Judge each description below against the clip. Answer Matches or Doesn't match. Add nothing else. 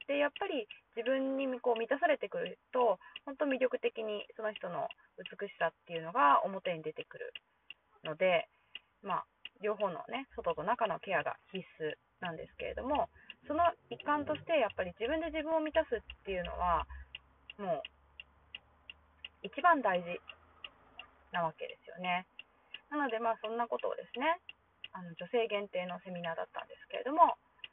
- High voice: Matches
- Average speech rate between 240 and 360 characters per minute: Matches